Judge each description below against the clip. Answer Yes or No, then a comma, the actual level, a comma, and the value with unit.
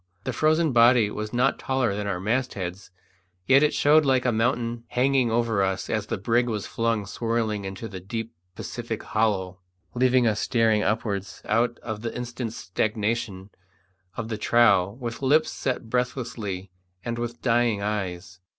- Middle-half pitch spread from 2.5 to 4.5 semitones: Yes, average, 3.0 semitones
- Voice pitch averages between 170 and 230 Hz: No, low, 115 Hz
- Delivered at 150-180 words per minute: Yes, average, 160 wpm